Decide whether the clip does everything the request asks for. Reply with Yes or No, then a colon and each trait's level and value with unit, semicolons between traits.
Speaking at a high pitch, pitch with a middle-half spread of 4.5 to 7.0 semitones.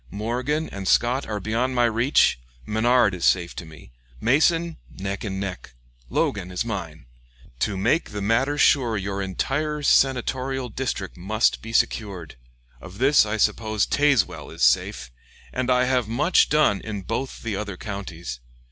No: low, 110 Hz; average, 4.8 semitones